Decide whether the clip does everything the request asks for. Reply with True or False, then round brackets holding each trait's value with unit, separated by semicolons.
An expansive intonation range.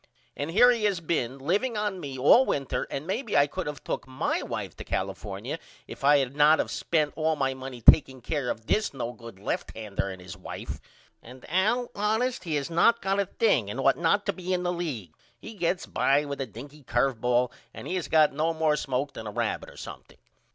True (6.1 semitones)